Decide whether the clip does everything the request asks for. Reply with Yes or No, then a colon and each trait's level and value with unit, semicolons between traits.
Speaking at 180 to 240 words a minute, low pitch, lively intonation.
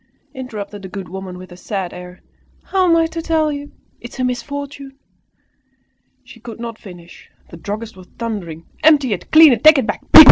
No: average, 190 wpm; high, 230 Hz; wide, 7.1 semitones